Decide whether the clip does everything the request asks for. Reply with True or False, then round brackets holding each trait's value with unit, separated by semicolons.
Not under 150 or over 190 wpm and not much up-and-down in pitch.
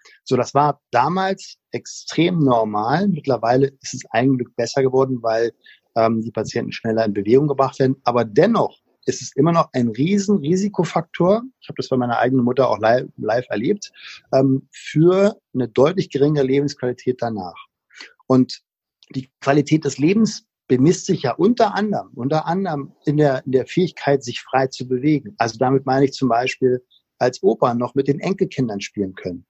False (170 wpm; 3.9 semitones)